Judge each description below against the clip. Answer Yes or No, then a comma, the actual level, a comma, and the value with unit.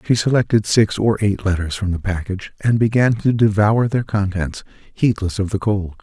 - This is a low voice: Yes, low, 105 Hz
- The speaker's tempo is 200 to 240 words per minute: No, average, 190 wpm